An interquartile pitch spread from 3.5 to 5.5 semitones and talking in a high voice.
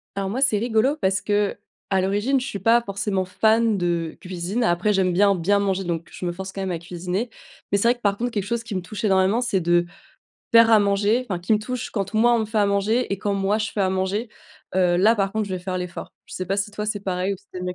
No: average, 2.8 semitones; high, 200 Hz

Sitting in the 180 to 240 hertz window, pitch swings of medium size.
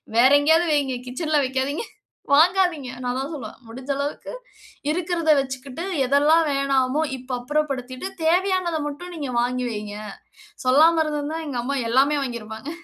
No: very high, 280 Hz; average, 3.8 semitones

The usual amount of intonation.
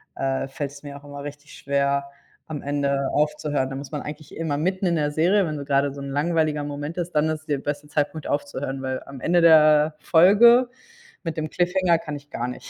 No: narrow, 2.2 semitones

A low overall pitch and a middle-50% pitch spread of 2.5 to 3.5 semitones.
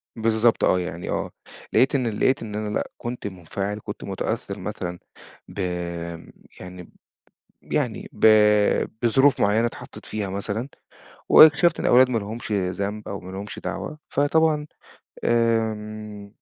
Yes: low, 110 Hz; average, 3.0 semitones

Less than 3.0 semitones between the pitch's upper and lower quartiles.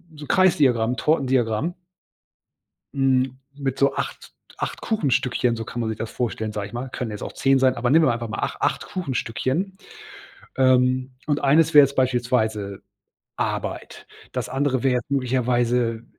Yes: narrow, 2.6 semitones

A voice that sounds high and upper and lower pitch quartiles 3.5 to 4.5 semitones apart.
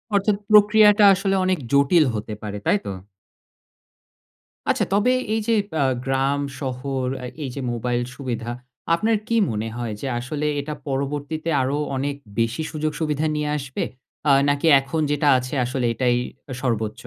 No: medium, 140 Hz; average, 4.1 semitones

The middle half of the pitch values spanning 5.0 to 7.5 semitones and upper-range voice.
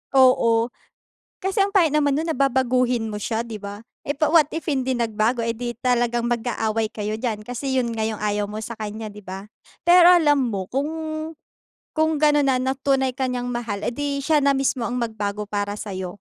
No: average, 4.1 semitones; high, 240 Hz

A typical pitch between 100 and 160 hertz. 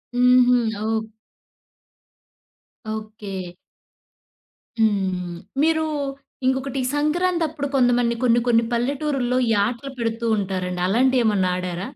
No: high, 240 Hz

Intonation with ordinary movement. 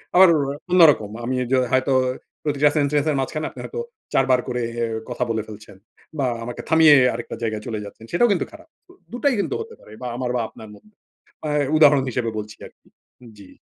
No: wide, 5.8 semitones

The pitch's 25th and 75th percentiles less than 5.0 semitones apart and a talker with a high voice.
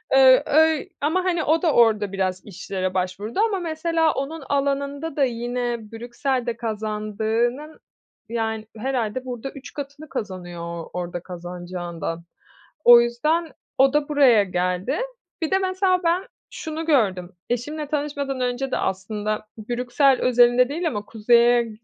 No: wide, 5.6 semitones; high, 245 Hz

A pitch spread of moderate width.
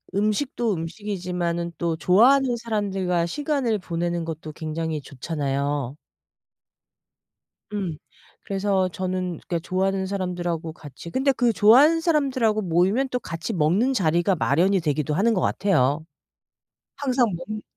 Yes: average, 4.7 semitones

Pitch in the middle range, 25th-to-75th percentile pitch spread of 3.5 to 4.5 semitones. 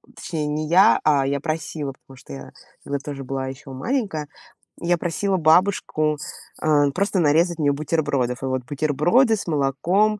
Yes: medium, 150 Hz; average, 3.9 semitones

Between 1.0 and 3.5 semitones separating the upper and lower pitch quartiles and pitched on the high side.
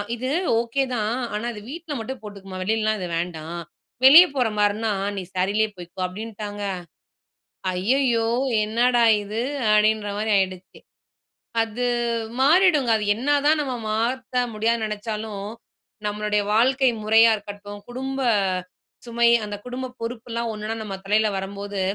Yes: average, 3.2 semitones; high, 220 Hz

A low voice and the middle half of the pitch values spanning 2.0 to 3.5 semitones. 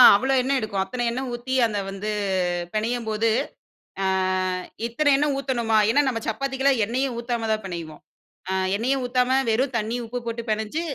No: high, 235 Hz; average, 3.2 semitones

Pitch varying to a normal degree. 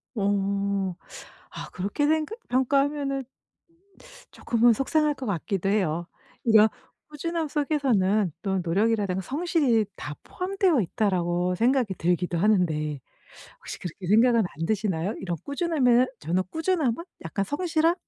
No: wide, 7.3 semitones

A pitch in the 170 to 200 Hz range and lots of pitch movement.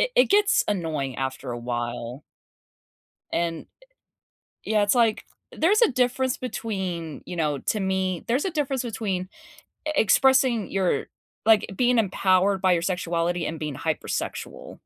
Yes: high, 190 Hz; wide, 6.8 semitones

